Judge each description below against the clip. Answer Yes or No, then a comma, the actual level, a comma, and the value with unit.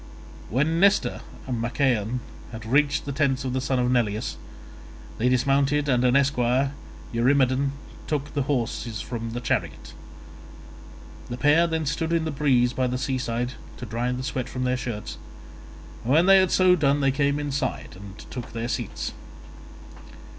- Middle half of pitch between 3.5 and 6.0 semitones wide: No, average, 2.9 semitones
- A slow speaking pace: No, average, 160 wpm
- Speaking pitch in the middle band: No, low, 130 Hz